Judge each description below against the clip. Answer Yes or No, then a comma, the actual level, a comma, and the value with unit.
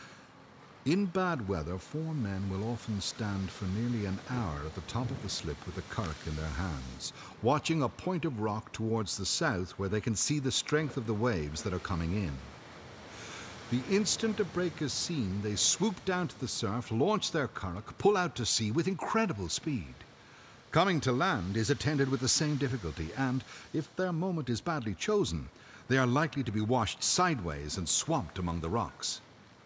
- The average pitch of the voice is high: No, low, 115 Hz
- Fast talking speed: No, average, 190 wpm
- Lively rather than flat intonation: Yes, wide, 7.9 semitones